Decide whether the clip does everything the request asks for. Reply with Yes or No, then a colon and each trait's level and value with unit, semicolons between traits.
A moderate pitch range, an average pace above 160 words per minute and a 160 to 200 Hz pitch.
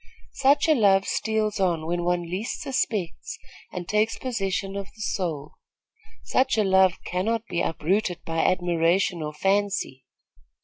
No: average, 3.5 semitones; average, 140 wpm; high, 190 Hz